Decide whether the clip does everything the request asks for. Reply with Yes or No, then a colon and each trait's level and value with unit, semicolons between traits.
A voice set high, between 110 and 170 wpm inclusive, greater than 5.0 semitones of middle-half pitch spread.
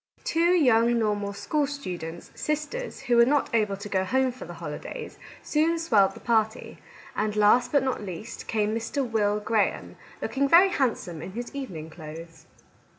Yes: high, 225 Hz; average, 165 wpm; wide, 5.6 semitones